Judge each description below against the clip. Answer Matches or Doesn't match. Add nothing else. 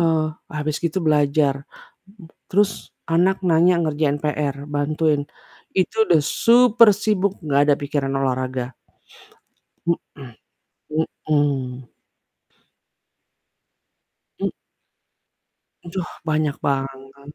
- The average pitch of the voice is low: Doesn't match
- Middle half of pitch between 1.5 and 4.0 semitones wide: Matches